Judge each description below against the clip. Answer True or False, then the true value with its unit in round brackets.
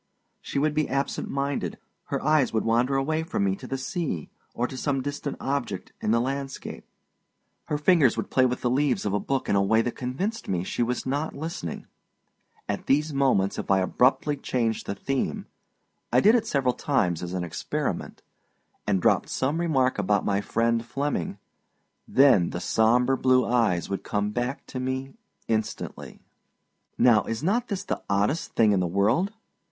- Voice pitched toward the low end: True (130 Hz)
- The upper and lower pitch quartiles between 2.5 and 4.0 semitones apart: False (5.0 semitones)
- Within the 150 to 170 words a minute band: False (180 wpm)